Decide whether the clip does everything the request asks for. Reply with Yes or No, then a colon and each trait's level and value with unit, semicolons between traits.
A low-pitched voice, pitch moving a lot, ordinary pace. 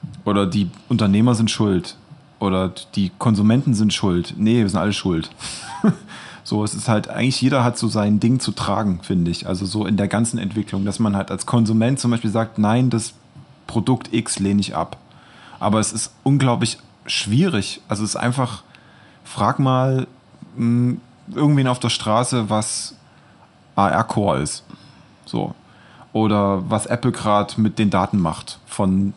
No: low, 110 Hz; average, 3.1 semitones; average, 165 wpm